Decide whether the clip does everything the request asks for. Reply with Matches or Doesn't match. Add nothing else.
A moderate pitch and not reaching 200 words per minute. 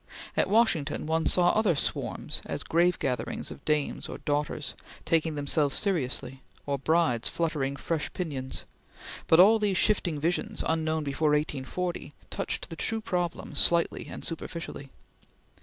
Matches